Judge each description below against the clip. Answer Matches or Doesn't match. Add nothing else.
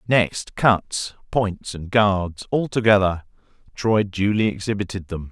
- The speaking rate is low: Matches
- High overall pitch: Doesn't match